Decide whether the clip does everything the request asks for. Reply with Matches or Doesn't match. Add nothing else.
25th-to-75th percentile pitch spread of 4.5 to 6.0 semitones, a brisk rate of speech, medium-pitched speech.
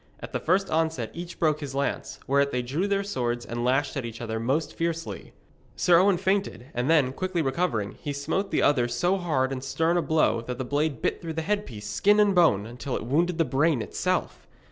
Matches